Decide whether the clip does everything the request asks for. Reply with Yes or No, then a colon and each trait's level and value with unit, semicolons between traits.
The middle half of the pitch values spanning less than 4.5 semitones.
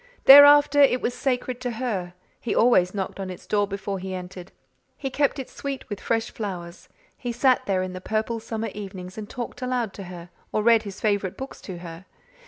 No: average, 5.0 semitones